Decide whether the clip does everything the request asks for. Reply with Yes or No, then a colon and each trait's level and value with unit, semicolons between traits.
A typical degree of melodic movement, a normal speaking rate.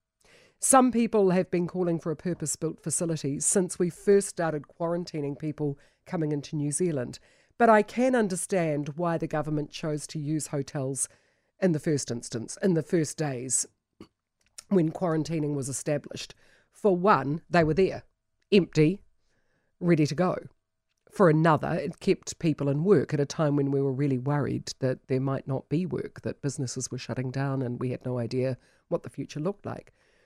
Yes: average, 4.3 semitones; average, 175 wpm